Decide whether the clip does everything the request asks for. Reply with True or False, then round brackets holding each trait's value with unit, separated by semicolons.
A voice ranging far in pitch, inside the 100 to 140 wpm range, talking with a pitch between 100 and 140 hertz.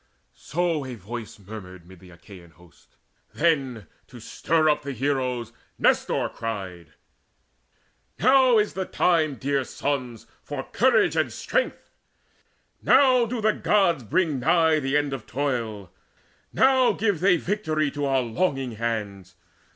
True (7.6 semitones; 135 wpm; 135 Hz)